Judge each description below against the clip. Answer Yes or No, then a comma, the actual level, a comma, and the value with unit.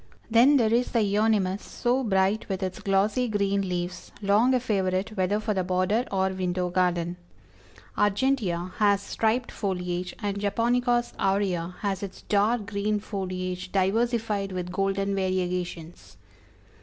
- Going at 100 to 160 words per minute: Yes, slow, 135 wpm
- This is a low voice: No, high, 195 Hz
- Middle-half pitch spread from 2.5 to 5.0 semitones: Yes, average, 2.8 semitones